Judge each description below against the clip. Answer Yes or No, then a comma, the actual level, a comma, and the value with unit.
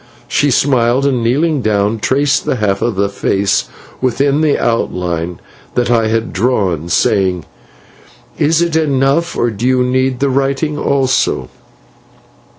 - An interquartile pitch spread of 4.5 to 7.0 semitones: Yes, average, 5.0 semitones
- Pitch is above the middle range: No, low, 125 Hz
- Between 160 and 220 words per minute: No, average, 140 wpm